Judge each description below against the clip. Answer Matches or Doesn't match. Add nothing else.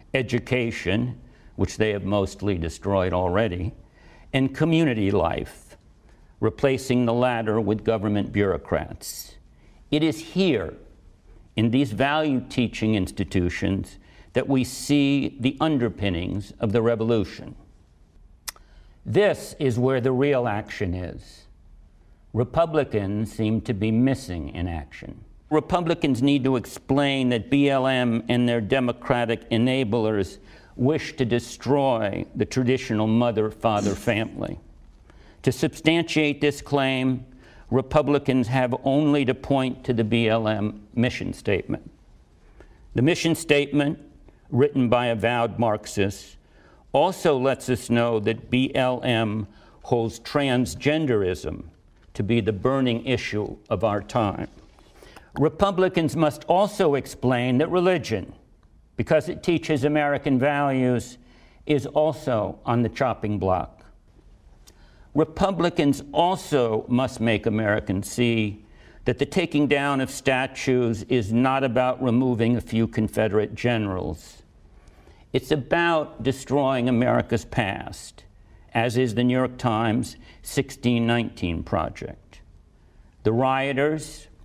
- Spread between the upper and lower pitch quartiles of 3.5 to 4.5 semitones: Matches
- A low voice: Matches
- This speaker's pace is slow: Matches